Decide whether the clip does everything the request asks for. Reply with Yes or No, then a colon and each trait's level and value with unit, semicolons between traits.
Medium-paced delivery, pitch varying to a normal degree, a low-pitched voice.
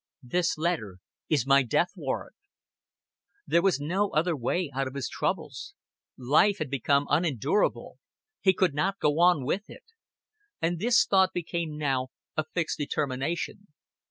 No: average, 145 wpm; average, 4.5 semitones; medium, 155 Hz